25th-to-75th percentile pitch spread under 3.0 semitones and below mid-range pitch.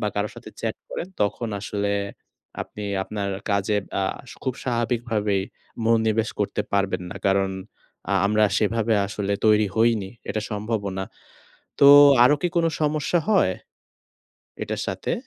Yes: narrow, 2.4 semitones; low, 105 Hz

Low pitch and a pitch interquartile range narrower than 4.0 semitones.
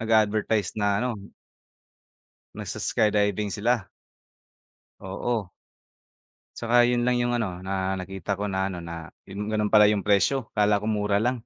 Yes: low, 105 Hz; narrow, 2.6 semitones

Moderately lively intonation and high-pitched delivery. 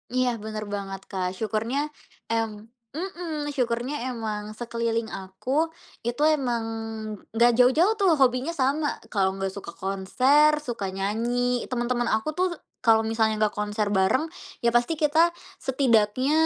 Yes: average, 3.6 semitones; high, 235 Hz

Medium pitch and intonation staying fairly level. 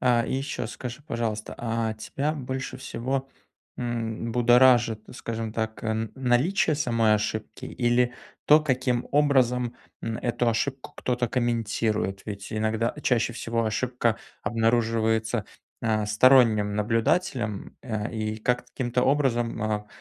No: low, 115 Hz; narrow, 2.2 semitones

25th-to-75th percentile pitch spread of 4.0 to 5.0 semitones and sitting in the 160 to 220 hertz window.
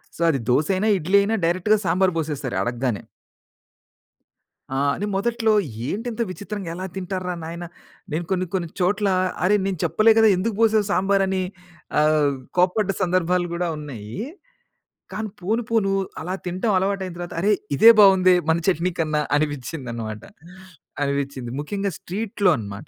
Yes: average, 4.6 semitones; medium, 185 Hz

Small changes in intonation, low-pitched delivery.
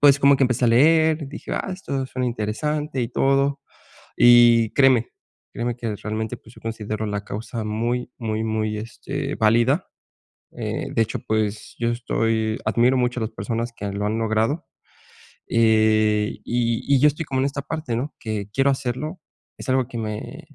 No: average, 3.7 semitones; low, 120 Hz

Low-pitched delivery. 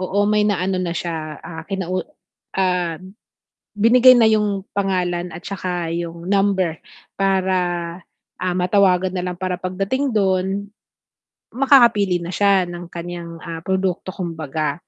No: medium, 185 Hz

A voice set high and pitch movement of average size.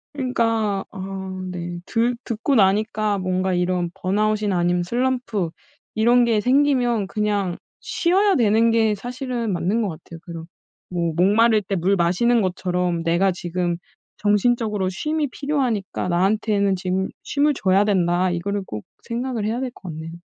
Yes: high, 205 Hz; average, 4.3 semitones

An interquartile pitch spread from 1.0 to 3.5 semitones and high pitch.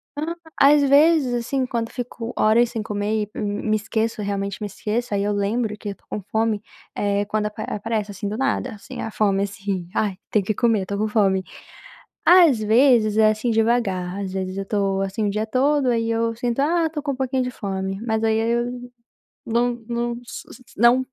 Yes: average, 3.0 semitones; high, 220 Hz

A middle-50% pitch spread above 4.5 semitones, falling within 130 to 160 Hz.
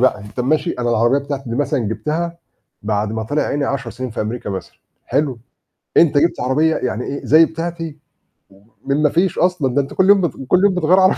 Yes: average, 5.2 semitones; medium, 140 Hz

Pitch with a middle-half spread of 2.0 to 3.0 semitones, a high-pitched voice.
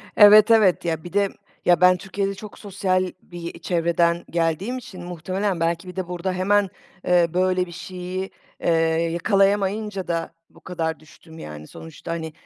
No: narrow, 2.6 semitones; medium, 180 Hz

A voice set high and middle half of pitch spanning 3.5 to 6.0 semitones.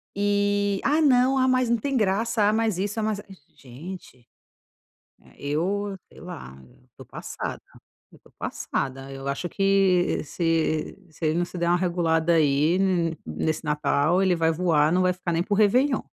No: medium, 180 Hz; average, 4.4 semitones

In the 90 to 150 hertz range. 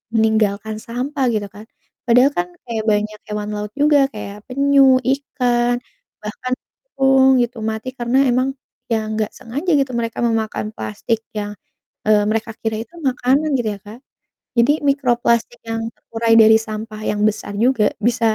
No: high, 230 Hz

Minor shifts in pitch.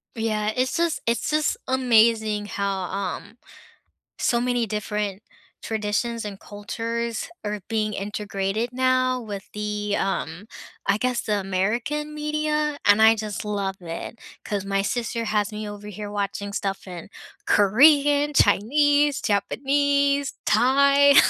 No: average, 4.1 semitones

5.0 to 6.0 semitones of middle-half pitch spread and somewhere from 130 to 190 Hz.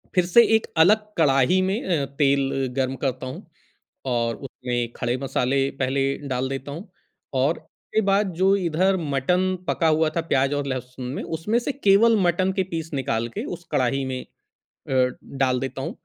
Yes: wide, 5.6 semitones; medium, 140 Hz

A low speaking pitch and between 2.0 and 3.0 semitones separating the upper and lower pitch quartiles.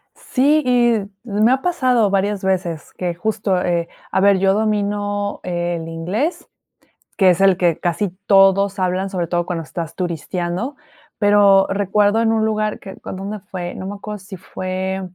No: high, 195 Hz; average, 2.7 semitones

